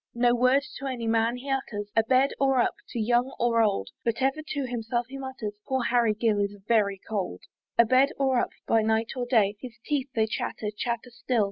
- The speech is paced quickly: Yes, fast, 215 wpm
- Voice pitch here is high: Yes, high, 240 Hz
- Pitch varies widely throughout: No, average, 2.8 semitones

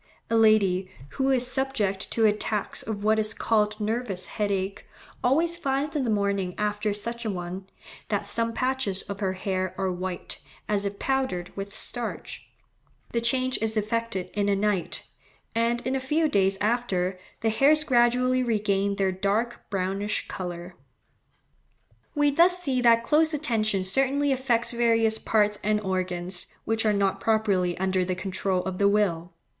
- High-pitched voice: Yes, high, 210 Hz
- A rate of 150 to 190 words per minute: Yes, average, 160 wpm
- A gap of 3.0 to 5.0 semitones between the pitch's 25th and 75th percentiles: Yes, average, 3.9 semitones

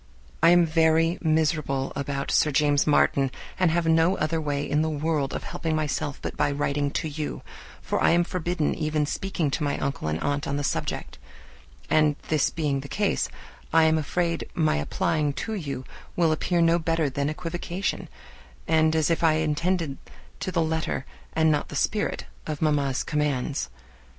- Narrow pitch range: Yes, narrow, 2.3 semitones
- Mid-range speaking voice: Yes, medium, 155 Hz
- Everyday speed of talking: Yes, average, 175 wpm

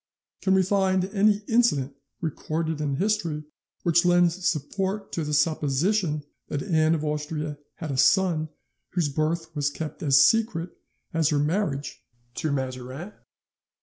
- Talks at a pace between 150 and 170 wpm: No, average, 140 wpm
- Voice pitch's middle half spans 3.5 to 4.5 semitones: Yes, average, 4.1 semitones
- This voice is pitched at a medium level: Yes, medium, 160 Hz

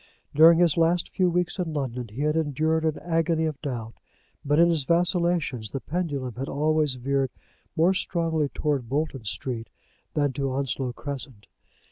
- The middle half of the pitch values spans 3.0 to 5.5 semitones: Yes, average, 3.6 semitones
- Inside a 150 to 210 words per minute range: Yes, average, 160 wpm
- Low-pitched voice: No, medium, 150 Hz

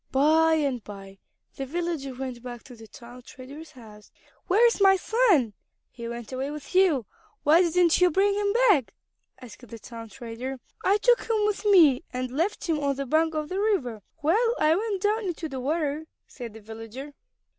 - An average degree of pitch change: No, wide, 6.5 semitones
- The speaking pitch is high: Yes, very high, 290 Hz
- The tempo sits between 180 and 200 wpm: Yes, average, 190 wpm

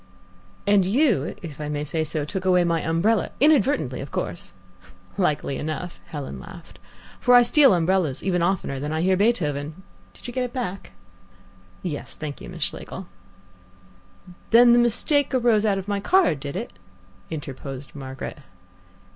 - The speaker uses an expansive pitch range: Yes, wide, 7.2 semitones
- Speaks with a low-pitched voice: No, medium, 180 Hz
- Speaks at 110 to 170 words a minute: Yes, average, 155 wpm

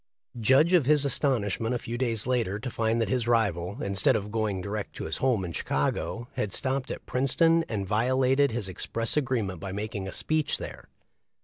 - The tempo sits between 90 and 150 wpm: No, average, 190 wpm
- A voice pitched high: No, low, 115 Hz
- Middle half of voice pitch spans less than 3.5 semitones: No, average, 4.5 semitones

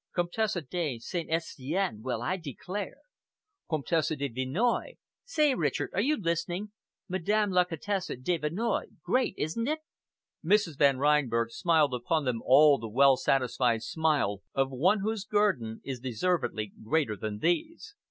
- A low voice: No, medium, 160 Hz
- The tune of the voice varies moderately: No, wide, 6.9 semitones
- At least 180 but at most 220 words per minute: No, average, 140 wpm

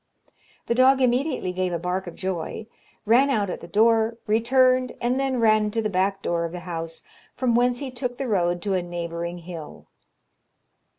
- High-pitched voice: Yes, high, 210 Hz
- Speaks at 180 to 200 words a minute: Yes, average, 185 wpm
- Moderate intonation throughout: No, wide, 5.7 semitones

